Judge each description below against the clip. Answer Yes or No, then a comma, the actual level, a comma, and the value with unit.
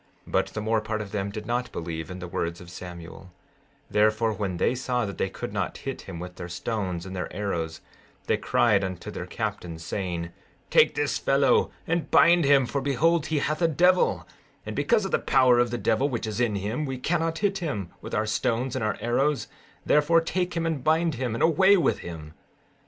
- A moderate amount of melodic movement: No, wide, 8.2 semitones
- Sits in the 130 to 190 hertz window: No, low, 115 Hz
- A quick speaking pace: Yes, fast, 210 wpm